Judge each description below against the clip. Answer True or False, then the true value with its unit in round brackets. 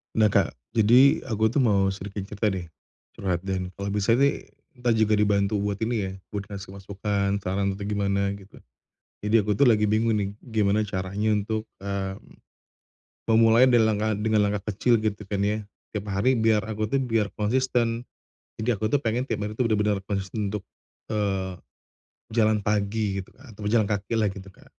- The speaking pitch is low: True (105 Hz)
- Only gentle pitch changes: True (2.0 semitones)